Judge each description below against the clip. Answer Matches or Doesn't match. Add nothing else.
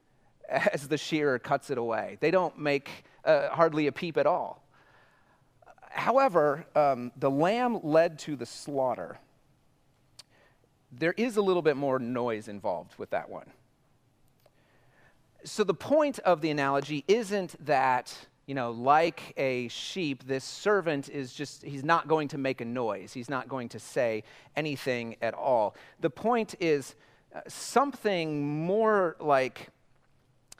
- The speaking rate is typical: Matches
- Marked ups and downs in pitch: Doesn't match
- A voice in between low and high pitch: Matches